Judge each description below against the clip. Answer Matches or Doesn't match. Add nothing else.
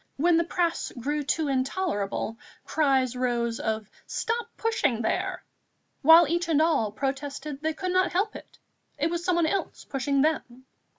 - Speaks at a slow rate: Doesn't match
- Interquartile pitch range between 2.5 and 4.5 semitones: Doesn't match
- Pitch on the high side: Matches